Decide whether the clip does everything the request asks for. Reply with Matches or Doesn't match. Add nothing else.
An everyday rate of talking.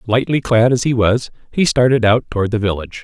Doesn't match